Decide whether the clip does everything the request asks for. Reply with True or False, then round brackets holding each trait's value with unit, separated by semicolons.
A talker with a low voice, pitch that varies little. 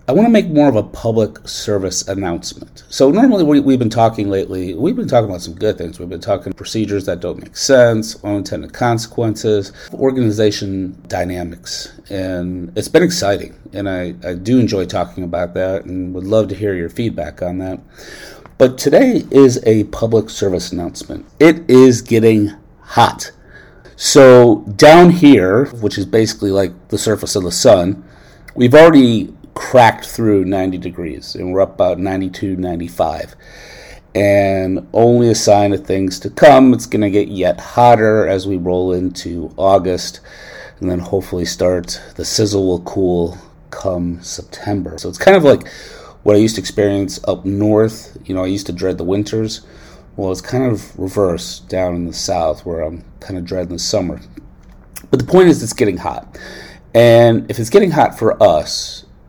False (100 Hz; 3.6 semitones)